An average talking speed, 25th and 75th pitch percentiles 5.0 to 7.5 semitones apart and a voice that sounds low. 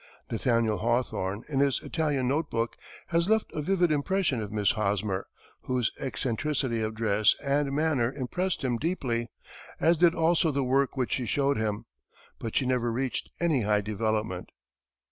Yes: average, 160 wpm; average, 5.3 semitones; low, 130 Hz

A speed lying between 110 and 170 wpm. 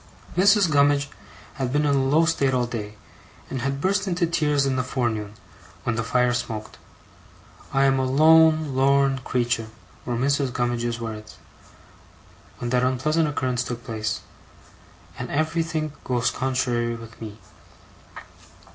Yes: average, 140 wpm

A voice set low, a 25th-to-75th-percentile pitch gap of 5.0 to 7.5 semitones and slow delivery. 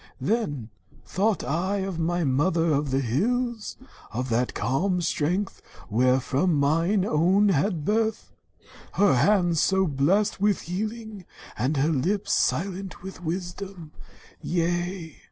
No: medium, 175 Hz; average, 5.3 semitones; slow, 125 wpm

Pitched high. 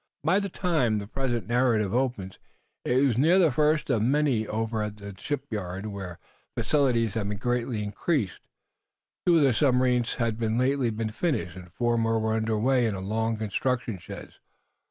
No: low, 115 Hz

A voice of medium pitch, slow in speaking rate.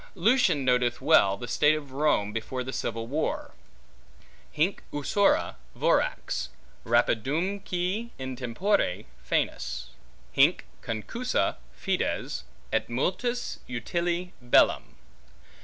Yes: medium, 145 Hz; slow, 95 wpm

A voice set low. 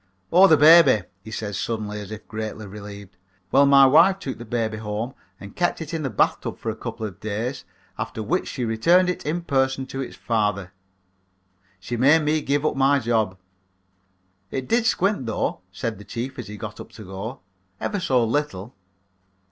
Yes: low, 120 Hz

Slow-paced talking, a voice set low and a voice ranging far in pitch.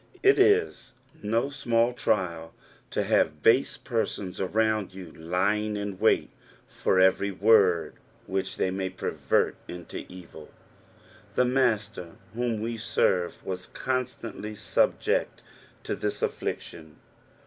No: slow, 115 wpm; low, 100 Hz; average, 4.0 semitones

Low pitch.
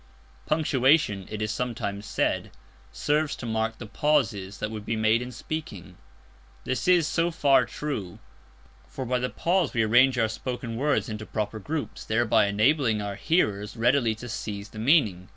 Yes: low, 115 Hz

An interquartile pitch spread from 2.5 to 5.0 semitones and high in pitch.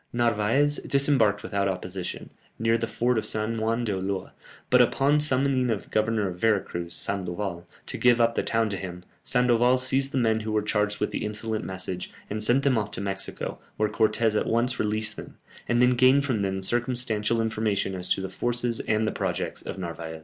No: average, 3.4 semitones; low, 110 Hz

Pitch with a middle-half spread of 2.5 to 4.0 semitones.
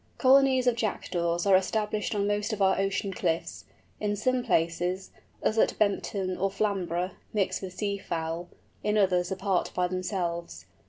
Yes: average, 2.8 semitones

